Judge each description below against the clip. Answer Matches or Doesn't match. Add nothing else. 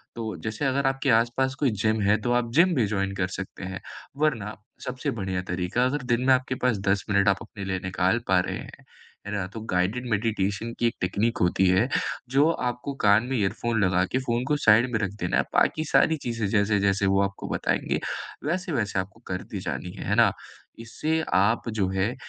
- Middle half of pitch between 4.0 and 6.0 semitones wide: Matches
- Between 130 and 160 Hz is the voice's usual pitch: Doesn't match